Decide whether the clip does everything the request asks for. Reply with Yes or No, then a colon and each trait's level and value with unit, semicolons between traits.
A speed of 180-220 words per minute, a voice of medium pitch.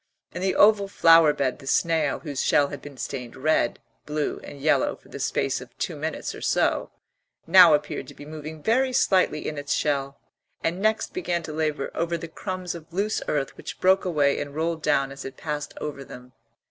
Yes: average, 200 wpm; medium, 155 Hz